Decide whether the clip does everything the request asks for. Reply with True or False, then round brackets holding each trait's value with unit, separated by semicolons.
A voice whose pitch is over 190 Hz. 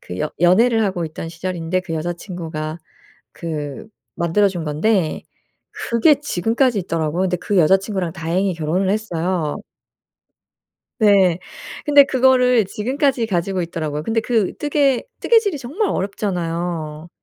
False (185 Hz)